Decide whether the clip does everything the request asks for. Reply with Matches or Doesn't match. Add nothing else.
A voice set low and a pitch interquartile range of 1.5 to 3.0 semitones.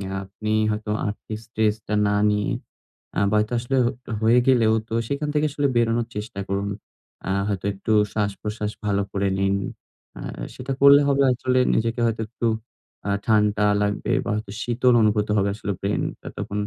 Matches